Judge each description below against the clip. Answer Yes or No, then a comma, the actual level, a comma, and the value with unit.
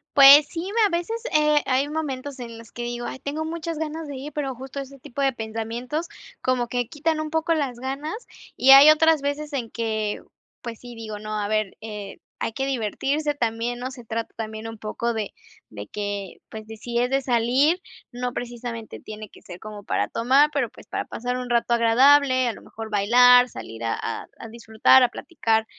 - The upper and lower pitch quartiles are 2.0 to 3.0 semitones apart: No, average, 4.1 semitones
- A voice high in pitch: Yes, high, 245 Hz